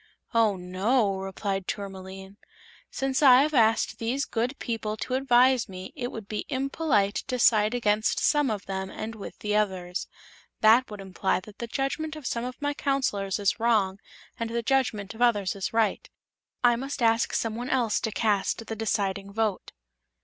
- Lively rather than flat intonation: No, average, 3.8 semitones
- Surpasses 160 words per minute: Yes, average, 170 wpm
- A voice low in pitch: No, high, 225 Hz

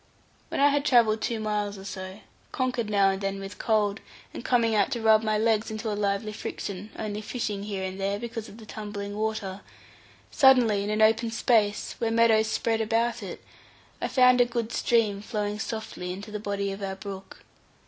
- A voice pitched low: No, high, 215 Hz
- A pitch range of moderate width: No, narrow, 2.0 semitones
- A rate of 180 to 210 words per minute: Yes, average, 200 wpm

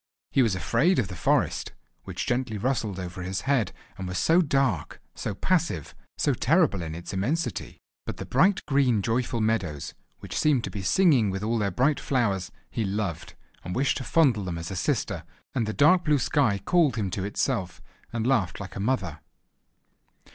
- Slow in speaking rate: No, average, 185 wpm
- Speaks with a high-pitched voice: No, low, 110 Hz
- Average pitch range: No, wide, 6.2 semitones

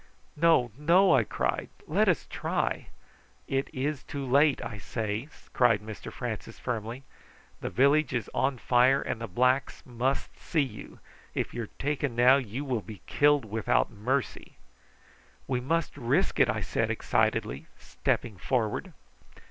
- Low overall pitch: Yes, low, 125 Hz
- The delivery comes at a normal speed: Yes, average, 150 wpm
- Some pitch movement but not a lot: Yes, average, 3.5 semitones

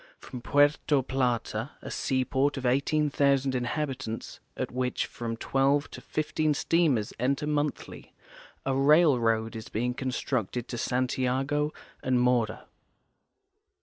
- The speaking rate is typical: No, slow, 115 wpm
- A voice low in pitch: Yes, low, 130 Hz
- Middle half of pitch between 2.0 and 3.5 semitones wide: Yes, average, 2.8 semitones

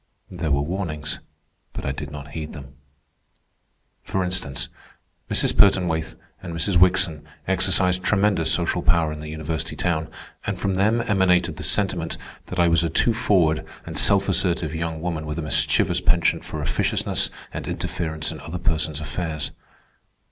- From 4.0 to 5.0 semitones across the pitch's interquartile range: No, average, 2.9 semitones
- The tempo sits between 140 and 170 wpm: Yes, average, 155 wpm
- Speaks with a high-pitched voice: No, very low, 85 Hz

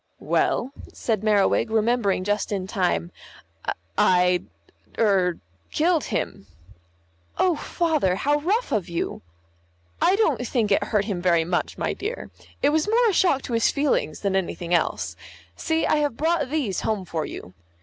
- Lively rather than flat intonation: Yes, wide, 8.5 semitones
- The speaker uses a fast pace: No, average, 155 wpm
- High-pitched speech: Yes, high, 220 Hz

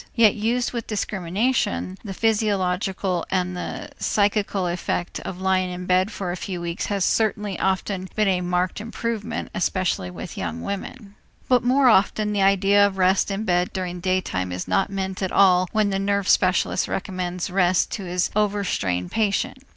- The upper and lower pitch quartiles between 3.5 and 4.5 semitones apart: No, narrow, 2.4 semitones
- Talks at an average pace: Yes, average, 170 wpm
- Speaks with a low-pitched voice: No, high, 190 Hz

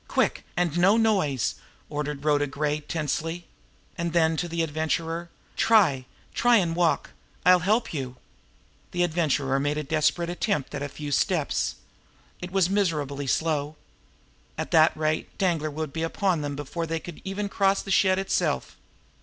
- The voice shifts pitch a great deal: No, average, 3.3 semitones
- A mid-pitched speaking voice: Yes, medium, 165 Hz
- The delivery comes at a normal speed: Yes, average, 155 wpm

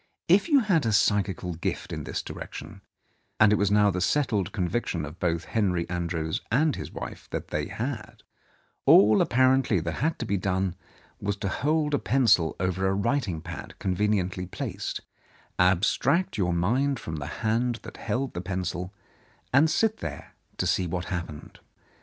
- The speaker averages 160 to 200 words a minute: Yes, average, 170 wpm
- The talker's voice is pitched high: No, low, 100 Hz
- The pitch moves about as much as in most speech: No, wide, 5.8 semitones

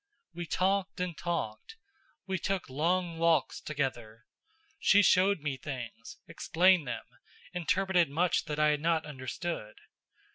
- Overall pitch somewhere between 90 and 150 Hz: No, medium, 165 Hz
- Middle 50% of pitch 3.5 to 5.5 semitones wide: Yes, average, 4.5 semitones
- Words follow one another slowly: Yes, slow, 130 wpm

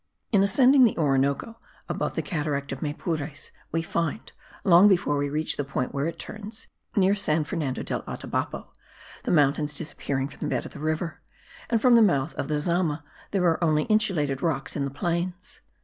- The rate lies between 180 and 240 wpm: Yes, average, 185 wpm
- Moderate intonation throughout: Yes, average, 4.6 semitones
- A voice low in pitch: No, medium, 160 Hz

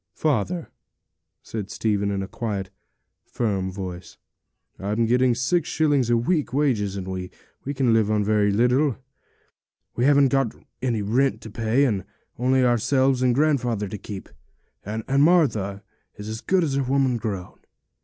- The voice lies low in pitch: Yes, low, 115 Hz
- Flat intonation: No, average, 4.7 semitones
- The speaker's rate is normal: Yes, average, 155 wpm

